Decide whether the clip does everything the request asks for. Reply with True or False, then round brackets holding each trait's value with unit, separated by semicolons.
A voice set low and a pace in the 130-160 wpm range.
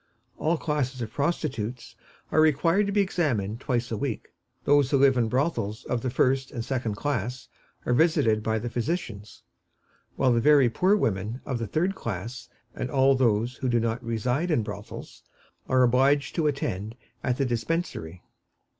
False (125 Hz; 170 wpm)